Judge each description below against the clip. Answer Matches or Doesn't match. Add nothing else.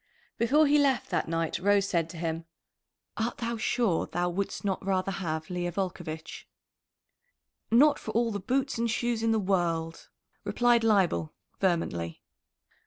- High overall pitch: Matches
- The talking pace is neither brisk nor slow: Matches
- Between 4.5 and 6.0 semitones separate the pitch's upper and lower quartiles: Matches